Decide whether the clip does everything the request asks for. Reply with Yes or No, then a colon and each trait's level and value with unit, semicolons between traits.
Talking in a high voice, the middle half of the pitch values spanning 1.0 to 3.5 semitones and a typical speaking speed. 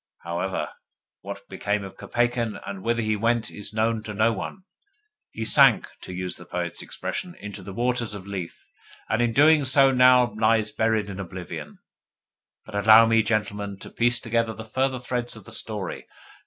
No: low, 110 Hz; average, 2.9 semitones; average, 170 wpm